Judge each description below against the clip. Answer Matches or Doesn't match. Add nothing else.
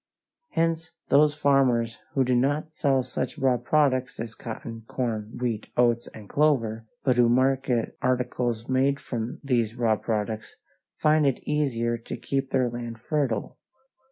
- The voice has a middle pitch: Doesn't match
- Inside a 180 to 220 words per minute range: Doesn't match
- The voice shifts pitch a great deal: Doesn't match